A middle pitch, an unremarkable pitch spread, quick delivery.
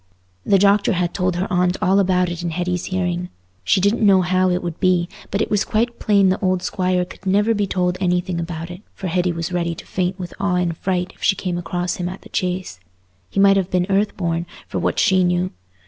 No: medium, 180 Hz; narrow, 1.5 semitones; fast, 235 wpm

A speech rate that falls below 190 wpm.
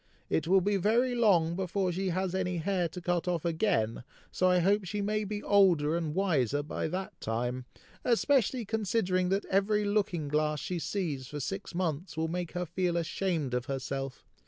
Yes: average, 180 wpm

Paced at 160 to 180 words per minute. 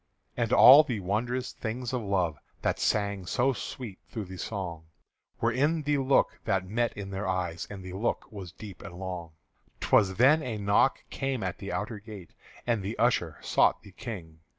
No: average, 190 wpm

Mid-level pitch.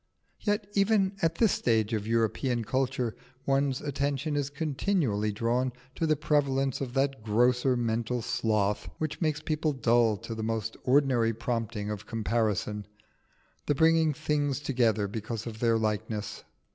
No: low, 125 Hz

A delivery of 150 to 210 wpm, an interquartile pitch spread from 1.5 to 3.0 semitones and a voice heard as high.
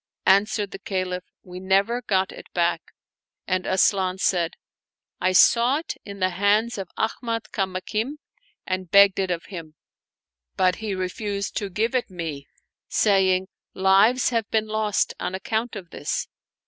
Yes: average, 160 wpm; average, 2.7 semitones; high, 195 Hz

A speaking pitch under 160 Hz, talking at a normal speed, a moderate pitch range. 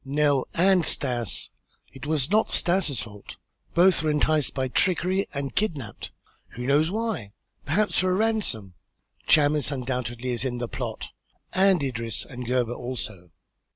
No: medium, 140 Hz; average, 145 wpm; wide, 6.2 semitones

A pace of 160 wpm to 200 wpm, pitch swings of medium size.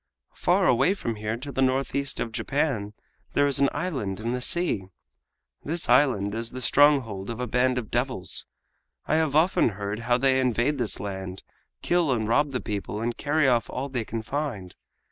Yes: average, 185 wpm; average, 4.4 semitones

